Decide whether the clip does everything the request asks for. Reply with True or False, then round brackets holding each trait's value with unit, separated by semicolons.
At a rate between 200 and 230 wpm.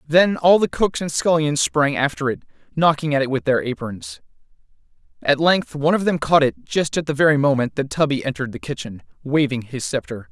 True (205 wpm)